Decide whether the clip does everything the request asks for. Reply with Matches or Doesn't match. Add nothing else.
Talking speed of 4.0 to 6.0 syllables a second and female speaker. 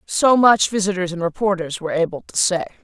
Matches